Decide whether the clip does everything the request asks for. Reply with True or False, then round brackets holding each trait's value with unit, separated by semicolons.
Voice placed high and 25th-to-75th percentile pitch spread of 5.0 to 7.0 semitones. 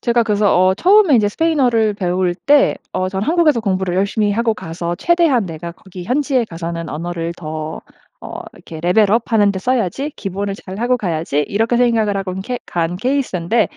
True (200 Hz; 5.3 semitones)